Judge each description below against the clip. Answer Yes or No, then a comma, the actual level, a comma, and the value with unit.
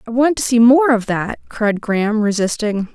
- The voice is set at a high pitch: Yes, high, 230 Hz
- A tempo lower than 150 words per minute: No, fast, 205 wpm